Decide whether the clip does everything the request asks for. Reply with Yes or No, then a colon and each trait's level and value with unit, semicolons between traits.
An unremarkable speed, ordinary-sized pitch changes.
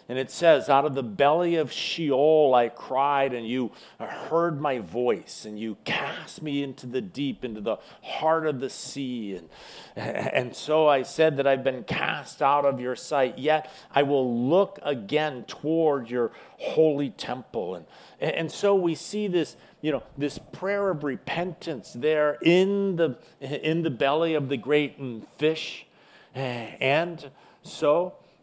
Yes: average, 160 wpm; average, 3.6 semitones